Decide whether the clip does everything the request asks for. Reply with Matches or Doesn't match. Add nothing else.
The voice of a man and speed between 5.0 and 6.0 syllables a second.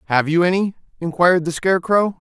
Doesn't match